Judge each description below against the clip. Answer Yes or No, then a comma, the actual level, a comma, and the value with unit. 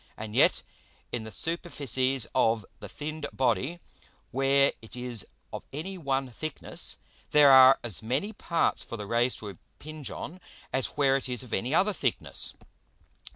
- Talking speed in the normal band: Yes, average, 155 wpm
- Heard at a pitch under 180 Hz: Yes, low, 135 Hz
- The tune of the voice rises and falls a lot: No, average, 4.1 semitones